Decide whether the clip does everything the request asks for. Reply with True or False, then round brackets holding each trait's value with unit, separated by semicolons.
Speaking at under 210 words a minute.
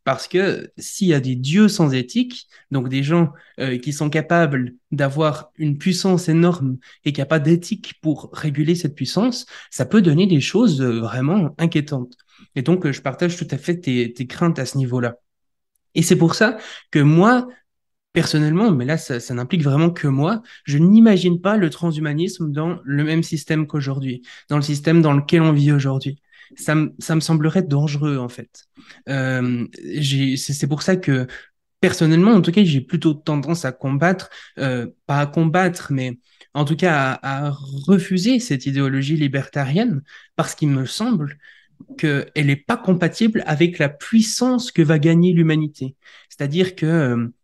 True (175 wpm)